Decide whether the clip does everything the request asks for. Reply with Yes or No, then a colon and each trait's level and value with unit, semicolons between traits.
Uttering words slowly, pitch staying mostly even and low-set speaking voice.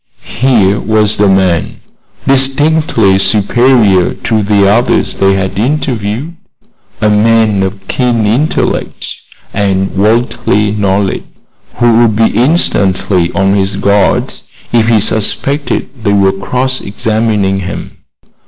No: slow, 115 wpm; average, 3.6 semitones; low, 105 Hz